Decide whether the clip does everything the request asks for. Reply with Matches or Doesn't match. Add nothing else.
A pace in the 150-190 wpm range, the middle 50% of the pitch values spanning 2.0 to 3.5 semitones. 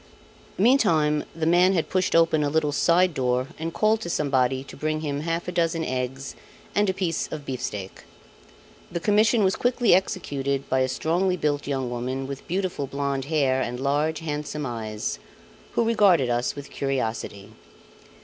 Doesn't match